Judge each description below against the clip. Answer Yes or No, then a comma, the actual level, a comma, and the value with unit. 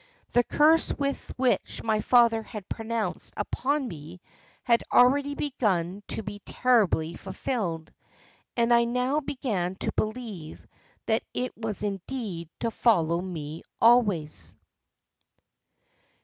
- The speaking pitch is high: Yes, high, 225 Hz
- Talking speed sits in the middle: No, slow, 110 wpm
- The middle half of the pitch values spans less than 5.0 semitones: No, wide, 5.5 semitones